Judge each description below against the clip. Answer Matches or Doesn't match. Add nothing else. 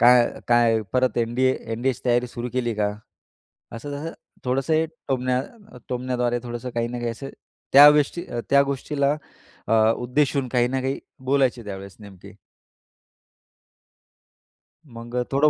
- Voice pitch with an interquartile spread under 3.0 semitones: Matches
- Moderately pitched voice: Doesn't match